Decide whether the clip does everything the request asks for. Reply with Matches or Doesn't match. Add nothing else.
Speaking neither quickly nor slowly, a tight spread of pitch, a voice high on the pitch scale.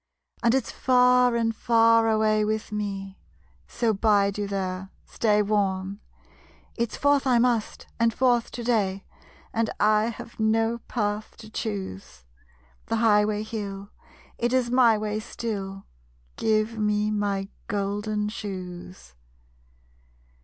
Doesn't match